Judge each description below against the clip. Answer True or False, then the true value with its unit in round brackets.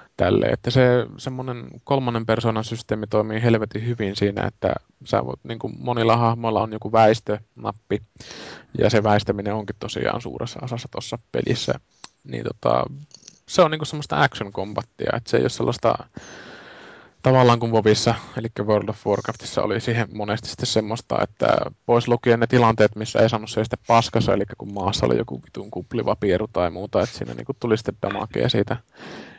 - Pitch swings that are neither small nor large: False (2.2 semitones)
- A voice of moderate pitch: False (115 Hz)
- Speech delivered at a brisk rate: True (160 wpm)